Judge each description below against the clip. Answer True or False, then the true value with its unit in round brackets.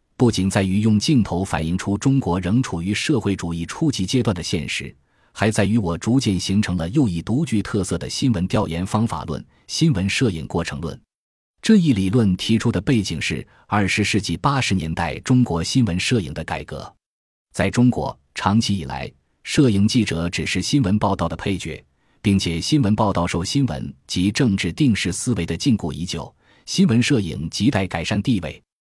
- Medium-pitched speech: False (100 Hz)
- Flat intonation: False (5.3 semitones)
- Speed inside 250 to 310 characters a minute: True (280 characters per minute)